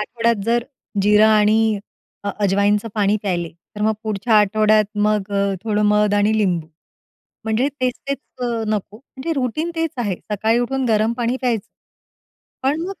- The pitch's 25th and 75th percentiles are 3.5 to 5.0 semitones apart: No, narrow, 2.4 semitones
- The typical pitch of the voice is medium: No, high, 215 Hz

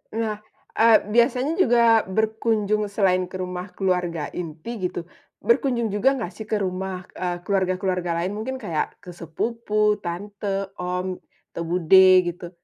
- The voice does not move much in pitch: No, average, 3.5 semitones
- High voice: Yes, high, 195 Hz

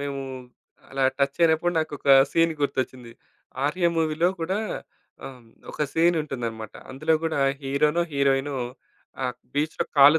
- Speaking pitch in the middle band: Yes, medium, 145 Hz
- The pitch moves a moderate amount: Yes, average, 3.1 semitones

